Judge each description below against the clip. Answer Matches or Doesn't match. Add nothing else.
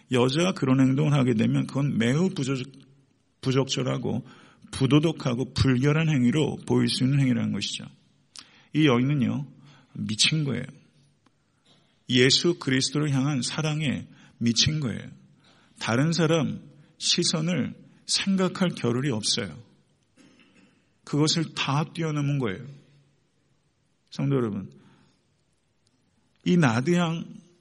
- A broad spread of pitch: Doesn't match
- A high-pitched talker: Doesn't match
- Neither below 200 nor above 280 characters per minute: Matches